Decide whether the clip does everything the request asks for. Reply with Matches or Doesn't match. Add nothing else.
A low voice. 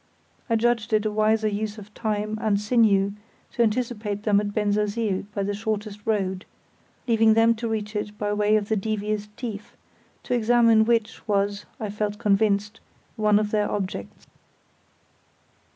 Doesn't match